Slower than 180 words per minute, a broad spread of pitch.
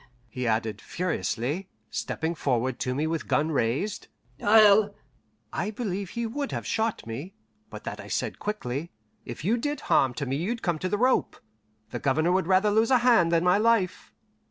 No: average, 185 wpm; wide, 7.5 semitones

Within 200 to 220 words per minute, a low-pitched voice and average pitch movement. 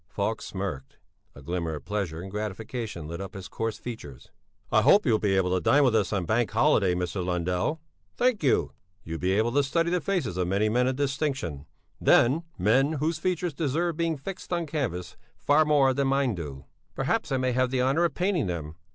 No: fast, 205 wpm; low, 115 Hz; wide, 8.1 semitones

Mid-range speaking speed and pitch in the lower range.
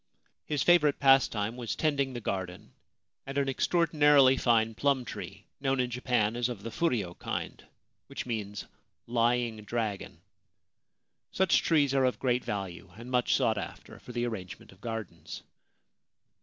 Yes: average, 155 wpm; low, 120 Hz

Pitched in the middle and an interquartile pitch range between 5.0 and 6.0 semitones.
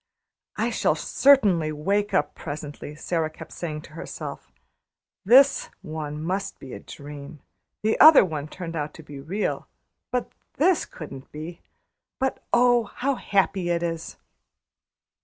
Yes: medium, 165 Hz; wide, 5.4 semitones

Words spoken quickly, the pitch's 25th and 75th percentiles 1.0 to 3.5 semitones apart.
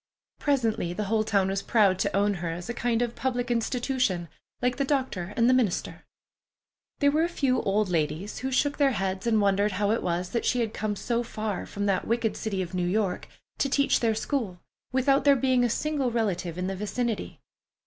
No: fast, 210 wpm; average, 4.6 semitones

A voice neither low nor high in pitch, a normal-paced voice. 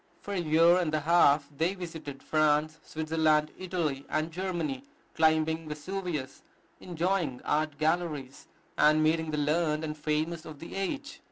Yes: medium, 155 Hz; average, 145 wpm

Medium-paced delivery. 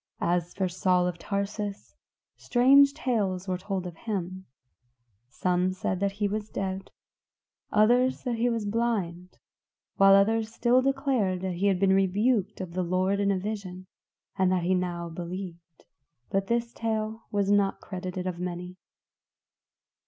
Yes: average, 150 wpm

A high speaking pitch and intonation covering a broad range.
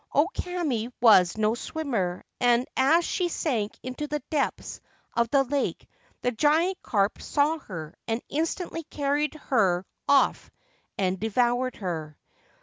Yes: very high, 250 Hz; wide, 5.8 semitones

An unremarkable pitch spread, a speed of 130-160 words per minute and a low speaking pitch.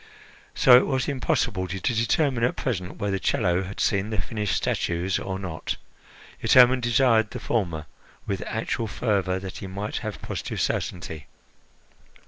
Yes: average, 4.2 semitones; average, 150 wpm; low, 100 Hz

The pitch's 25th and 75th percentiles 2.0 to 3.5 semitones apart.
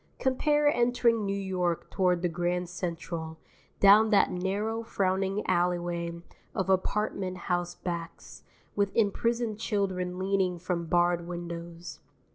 Yes: narrow, 2.6 semitones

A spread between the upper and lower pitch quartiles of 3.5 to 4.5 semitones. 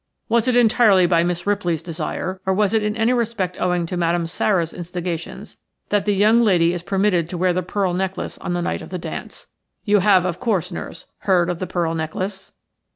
No: average, 2.9 semitones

